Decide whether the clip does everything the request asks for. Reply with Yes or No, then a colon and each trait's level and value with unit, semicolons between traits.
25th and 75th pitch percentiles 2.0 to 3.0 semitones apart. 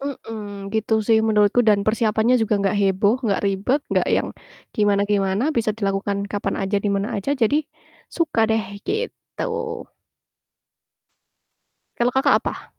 Yes: average, 2.7 semitones